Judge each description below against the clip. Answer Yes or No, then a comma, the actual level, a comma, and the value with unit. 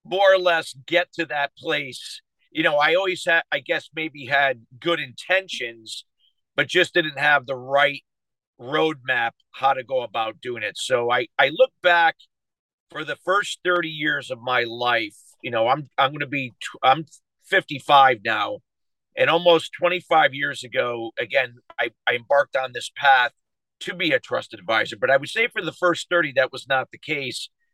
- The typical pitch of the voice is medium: Yes, medium, 150 Hz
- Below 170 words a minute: No, average, 180 wpm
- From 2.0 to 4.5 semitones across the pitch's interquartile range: No, average, 4.9 semitones